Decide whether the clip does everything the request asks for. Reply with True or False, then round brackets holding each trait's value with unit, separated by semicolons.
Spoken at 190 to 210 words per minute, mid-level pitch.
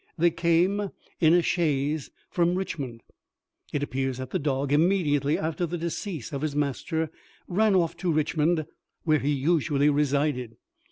False (150 wpm; 155 Hz)